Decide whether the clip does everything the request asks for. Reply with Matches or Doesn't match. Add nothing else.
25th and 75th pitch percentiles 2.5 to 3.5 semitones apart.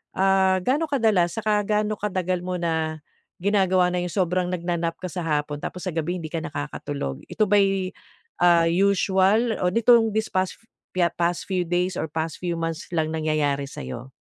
Matches